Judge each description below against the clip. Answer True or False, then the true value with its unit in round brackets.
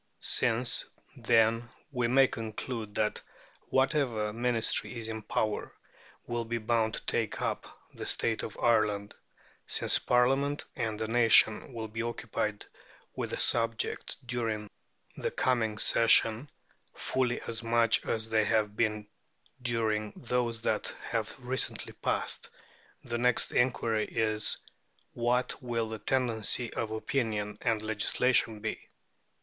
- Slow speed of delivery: True (125 wpm)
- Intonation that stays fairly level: True (1.9 semitones)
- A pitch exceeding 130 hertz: False (115 Hz)